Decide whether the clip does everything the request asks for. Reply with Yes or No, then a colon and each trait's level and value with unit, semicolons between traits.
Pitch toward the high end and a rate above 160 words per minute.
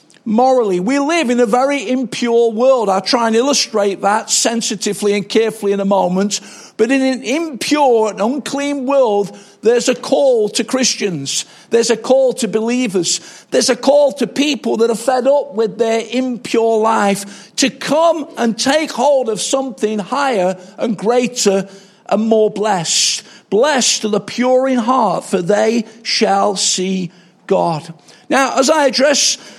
No: high, 230 Hz; average, 155 wpm